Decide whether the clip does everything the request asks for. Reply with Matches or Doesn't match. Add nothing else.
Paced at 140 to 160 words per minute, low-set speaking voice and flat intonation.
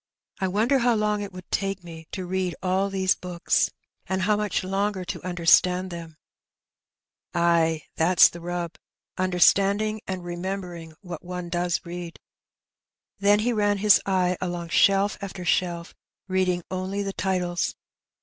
Doesn't match